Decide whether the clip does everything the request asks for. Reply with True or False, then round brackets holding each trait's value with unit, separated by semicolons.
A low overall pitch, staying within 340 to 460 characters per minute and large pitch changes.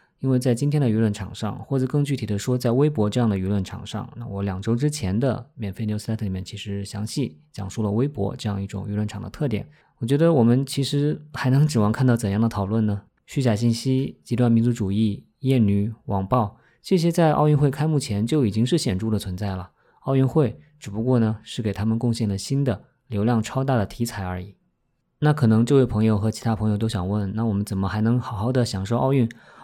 False (115 Hz; 350 characters per minute; 4.1 semitones)